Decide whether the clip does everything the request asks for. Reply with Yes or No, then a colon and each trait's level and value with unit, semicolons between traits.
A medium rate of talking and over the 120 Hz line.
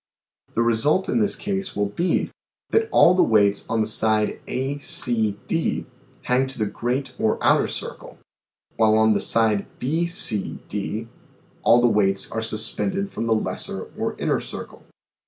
No: average, 170 wpm; low, 115 Hz